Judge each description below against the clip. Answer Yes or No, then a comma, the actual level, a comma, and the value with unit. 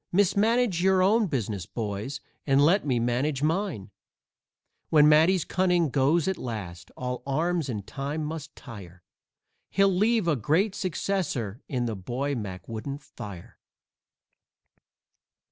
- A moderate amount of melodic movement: No, wide, 7.5 semitones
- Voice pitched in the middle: Yes, medium, 145 Hz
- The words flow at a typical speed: No, slow, 130 wpm